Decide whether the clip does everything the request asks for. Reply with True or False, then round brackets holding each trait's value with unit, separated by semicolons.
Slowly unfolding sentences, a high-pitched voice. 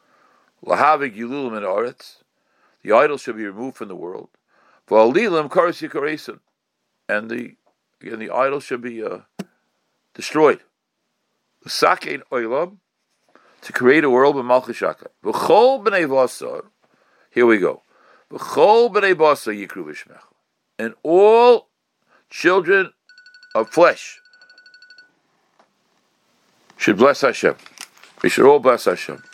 True (115 wpm; 225 Hz)